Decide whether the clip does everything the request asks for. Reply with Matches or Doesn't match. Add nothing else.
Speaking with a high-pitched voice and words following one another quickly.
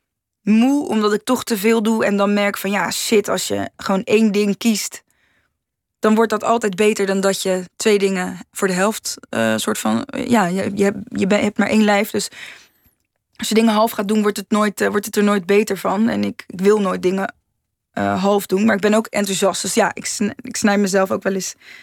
Matches